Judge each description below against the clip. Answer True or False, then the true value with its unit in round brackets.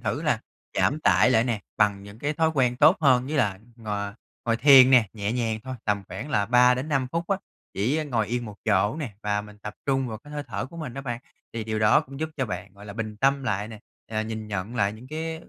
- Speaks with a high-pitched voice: False (115 Hz)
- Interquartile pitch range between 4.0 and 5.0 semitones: True (4.5 semitones)